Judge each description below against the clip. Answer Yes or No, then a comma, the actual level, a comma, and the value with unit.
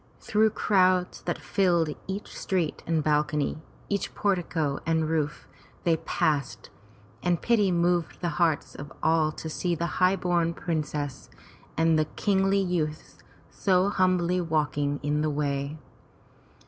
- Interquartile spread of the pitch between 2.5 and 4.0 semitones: Yes, average, 3.3 semitones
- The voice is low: No, medium, 165 Hz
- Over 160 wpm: No, slow, 135 wpm